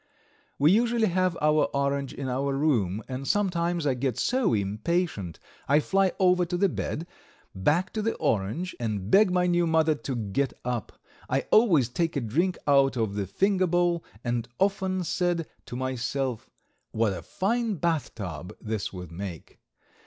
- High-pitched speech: No, medium, 145 Hz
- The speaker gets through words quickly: No, average, 160 wpm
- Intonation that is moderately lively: No, wide, 7.6 semitones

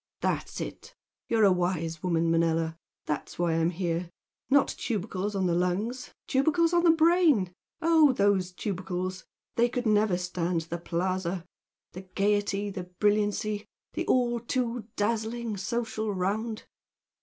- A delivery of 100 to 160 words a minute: Yes, average, 140 wpm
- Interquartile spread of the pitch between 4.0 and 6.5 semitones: Yes, average, 4.6 semitones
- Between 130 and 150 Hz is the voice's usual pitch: No, high, 200 Hz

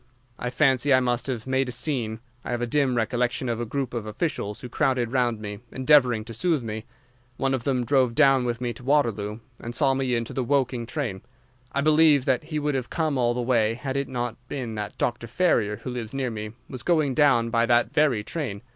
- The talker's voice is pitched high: No, low, 125 Hz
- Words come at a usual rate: No, fast, 225 wpm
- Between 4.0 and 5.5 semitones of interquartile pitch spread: No, average, 2.7 semitones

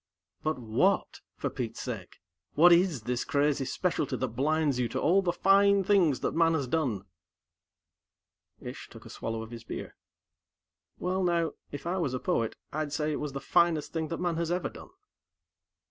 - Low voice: No, medium, 155 Hz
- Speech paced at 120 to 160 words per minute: No, average, 180 wpm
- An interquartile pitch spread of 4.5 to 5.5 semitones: Yes, average, 5.2 semitones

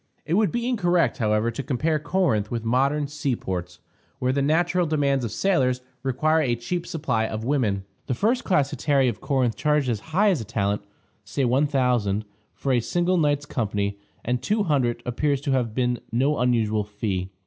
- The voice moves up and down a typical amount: Yes, average, 4.9 semitones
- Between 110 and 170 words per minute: No, average, 180 wpm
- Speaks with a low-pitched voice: Yes, low, 130 Hz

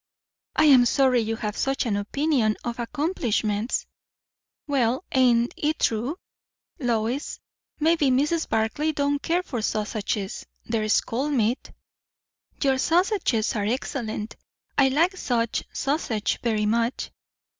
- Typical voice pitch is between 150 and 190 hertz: No, high, 245 Hz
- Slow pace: Yes, slow, 120 wpm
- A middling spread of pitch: Yes, average, 4.6 semitones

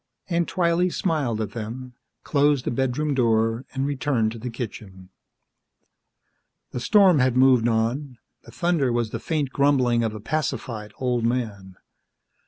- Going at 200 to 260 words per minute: No, average, 145 wpm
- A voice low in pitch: Yes, low, 125 Hz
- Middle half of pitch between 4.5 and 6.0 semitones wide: No, average, 4.1 semitones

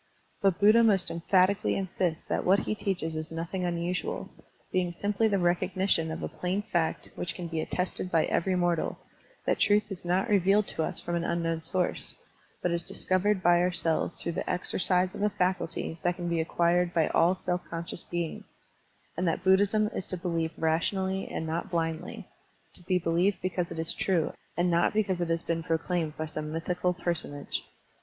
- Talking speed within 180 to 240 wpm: Yes, average, 185 wpm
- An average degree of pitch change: No, narrow, 2.1 semitones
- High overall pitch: No, medium, 175 Hz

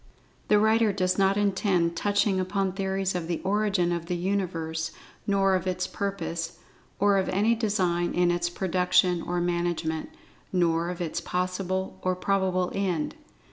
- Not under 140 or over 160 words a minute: Yes, average, 150 wpm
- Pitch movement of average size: No, narrow, 2.2 semitones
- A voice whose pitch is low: No, medium, 185 Hz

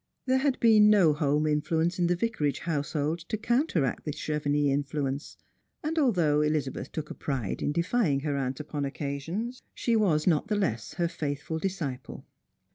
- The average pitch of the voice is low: No, medium, 155 Hz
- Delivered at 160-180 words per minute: Yes, average, 165 wpm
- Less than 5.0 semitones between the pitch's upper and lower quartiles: No, average, 5.3 semitones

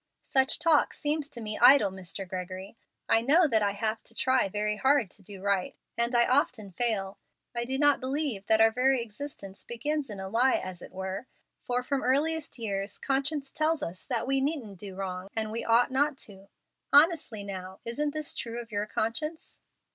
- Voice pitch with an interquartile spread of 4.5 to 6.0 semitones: Yes, wide, 5.6 semitones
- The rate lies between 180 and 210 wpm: Yes, average, 190 wpm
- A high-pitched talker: Yes, high, 235 Hz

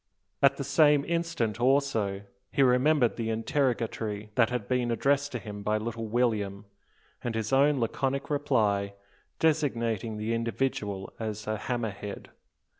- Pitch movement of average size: Yes, average, 4.3 semitones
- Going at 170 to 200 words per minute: No, average, 140 wpm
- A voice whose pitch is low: Yes, low, 115 Hz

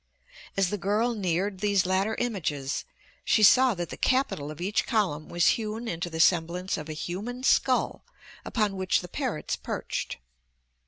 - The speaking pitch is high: Yes, high, 195 Hz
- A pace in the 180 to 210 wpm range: No, average, 160 wpm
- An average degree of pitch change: Yes, average, 4.2 semitones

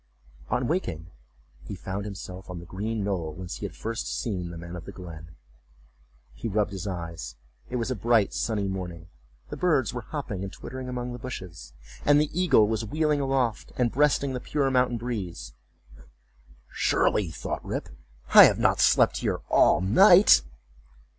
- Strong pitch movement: Yes, wide, 5.9 semitones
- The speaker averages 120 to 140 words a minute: No, average, 170 wpm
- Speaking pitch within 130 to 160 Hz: No, low, 105 Hz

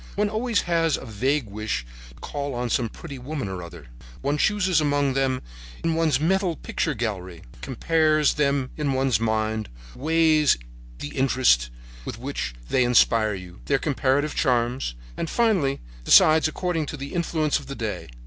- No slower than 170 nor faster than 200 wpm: No, average, 160 wpm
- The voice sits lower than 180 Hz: Yes, medium, 140 Hz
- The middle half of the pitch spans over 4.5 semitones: Yes, average, 5.3 semitones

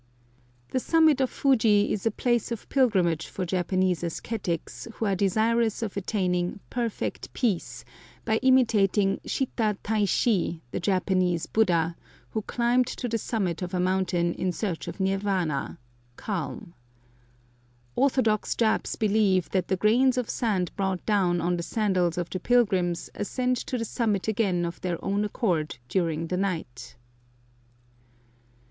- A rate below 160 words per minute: Yes, average, 140 wpm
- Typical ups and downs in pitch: Yes, average, 4.0 semitones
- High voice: Yes, high, 195 Hz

